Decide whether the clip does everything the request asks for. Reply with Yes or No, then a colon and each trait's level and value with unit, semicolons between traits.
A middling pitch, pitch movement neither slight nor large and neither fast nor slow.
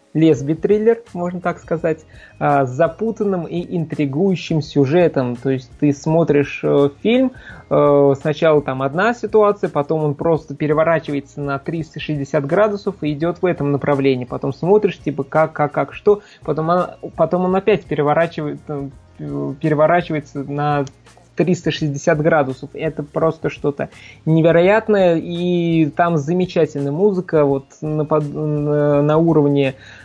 Yes: medium, 155 Hz; average, 3.4 semitones; average, 120 wpm